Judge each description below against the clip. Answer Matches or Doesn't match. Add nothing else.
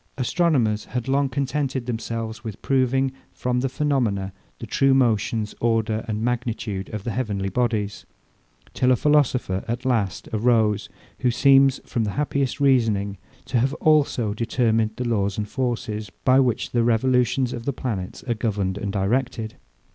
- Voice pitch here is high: Doesn't match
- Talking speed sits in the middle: Matches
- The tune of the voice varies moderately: Matches